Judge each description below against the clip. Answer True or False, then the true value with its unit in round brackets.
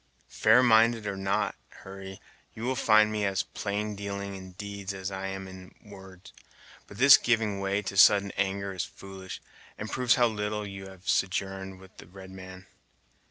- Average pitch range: False (1.7 semitones)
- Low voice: True (100 Hz)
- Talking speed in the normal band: True (170 wpm)